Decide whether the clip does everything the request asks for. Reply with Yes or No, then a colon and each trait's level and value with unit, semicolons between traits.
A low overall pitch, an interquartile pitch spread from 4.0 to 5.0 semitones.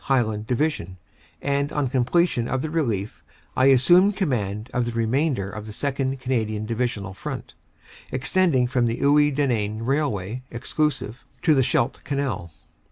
Yes: low, 125 Hz; average, 4.4 semitones